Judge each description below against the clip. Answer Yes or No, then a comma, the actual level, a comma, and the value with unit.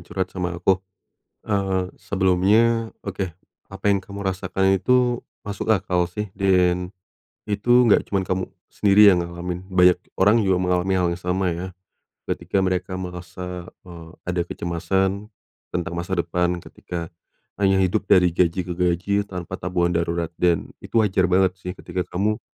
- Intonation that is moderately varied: No, narrow, 1.7 semitones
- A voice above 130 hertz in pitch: No, very low, 95 Hz